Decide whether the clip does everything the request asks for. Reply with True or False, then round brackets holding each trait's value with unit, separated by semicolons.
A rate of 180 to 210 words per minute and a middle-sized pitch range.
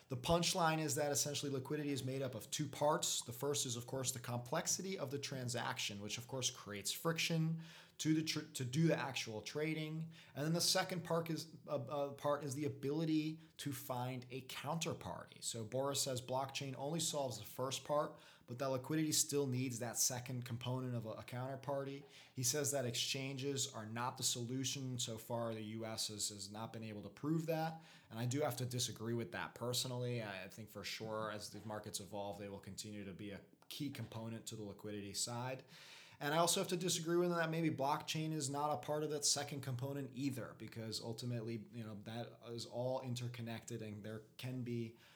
True (200 wpm; 4.6 semitones)